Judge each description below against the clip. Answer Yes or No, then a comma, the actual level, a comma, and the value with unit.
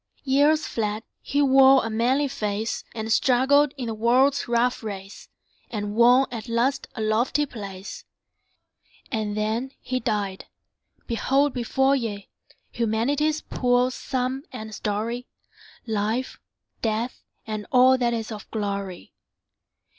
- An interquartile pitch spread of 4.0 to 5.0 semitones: No, average, 3.5 semitones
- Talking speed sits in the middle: No, slow, 125 wpm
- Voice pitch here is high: Yes, high, 235 Hz